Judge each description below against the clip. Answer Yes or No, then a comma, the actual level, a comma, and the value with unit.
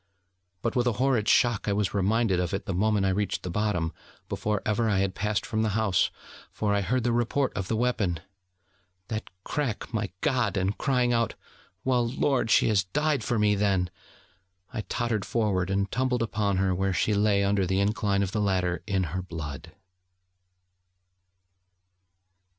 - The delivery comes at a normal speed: Yes, average, 175 wpm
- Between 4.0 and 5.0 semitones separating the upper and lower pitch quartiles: No, average, 3.3 semitones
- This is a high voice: No, low, 105 Hz